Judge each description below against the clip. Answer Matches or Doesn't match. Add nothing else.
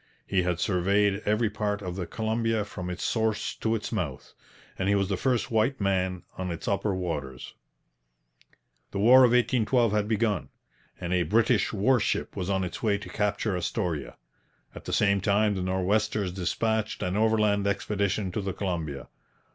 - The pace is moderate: Matches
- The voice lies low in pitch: Matches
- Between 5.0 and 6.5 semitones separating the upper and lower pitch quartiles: Doesn't match